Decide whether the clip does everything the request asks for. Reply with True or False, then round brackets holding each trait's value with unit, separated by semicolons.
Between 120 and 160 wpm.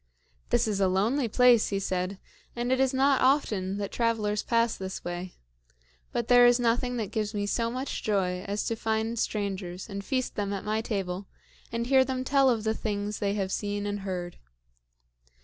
False (190 wpm)